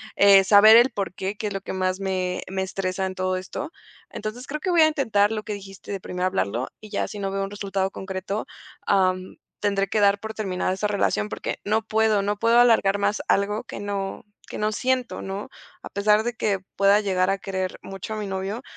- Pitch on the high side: Yes, high, 200 Hz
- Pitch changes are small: Yes, narrow, 2.0 semitones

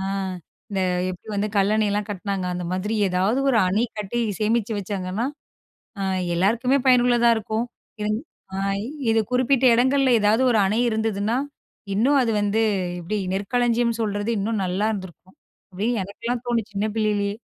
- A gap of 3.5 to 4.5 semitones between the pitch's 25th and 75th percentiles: No, average, 3.0 semitones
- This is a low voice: No, high, 215 Hz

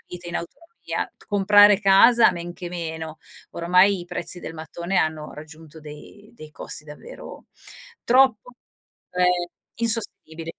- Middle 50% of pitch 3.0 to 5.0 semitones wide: Yes, average, 4.1 semitones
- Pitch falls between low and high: Yes, medium, 175 Hz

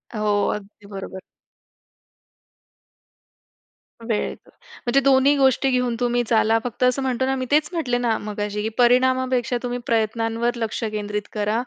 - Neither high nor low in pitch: No, high, 240 Hz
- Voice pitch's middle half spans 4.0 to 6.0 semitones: No, average, 3.1 semitones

